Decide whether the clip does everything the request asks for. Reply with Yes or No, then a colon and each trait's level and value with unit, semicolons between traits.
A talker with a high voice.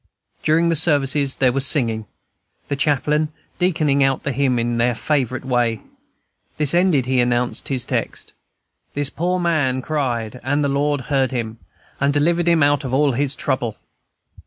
No: medium, 140 Hz